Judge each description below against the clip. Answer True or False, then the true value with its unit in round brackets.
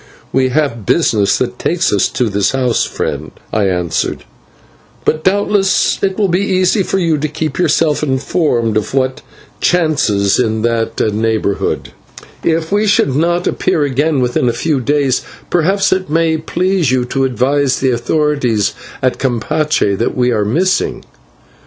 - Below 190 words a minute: True (155 wpm)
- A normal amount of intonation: False (5.8 semitones)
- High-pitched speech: False (140 Hz)